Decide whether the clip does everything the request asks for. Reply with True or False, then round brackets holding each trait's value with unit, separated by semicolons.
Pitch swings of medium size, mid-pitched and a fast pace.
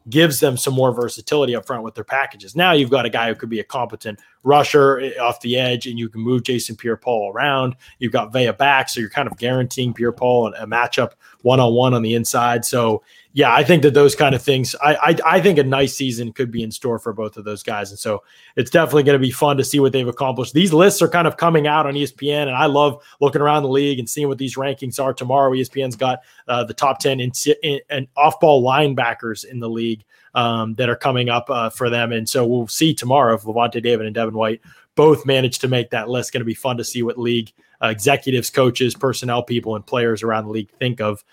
False (3.0 semitones; 125 Hz; 255 wpm)